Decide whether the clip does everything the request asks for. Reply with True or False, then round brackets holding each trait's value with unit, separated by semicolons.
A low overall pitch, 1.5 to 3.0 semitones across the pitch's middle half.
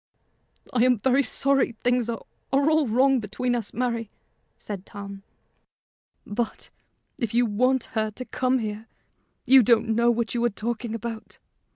False (235 Hz; 2.5 semitones)